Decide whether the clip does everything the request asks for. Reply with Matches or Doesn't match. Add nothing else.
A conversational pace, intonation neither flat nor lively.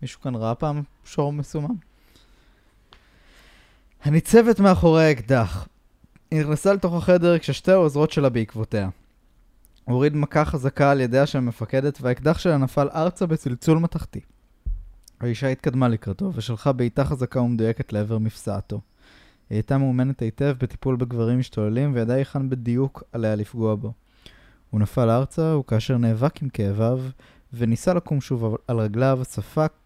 Matches